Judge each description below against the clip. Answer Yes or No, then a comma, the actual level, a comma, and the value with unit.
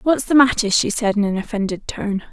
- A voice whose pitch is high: Yes, high, 220 Hz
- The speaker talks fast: Yes, fast, 235 wpm